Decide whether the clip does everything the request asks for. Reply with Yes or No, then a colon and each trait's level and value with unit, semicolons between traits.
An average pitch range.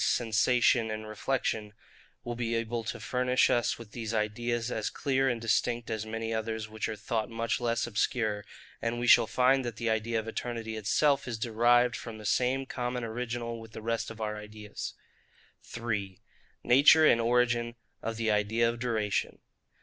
No: narrow, 1.7 semitones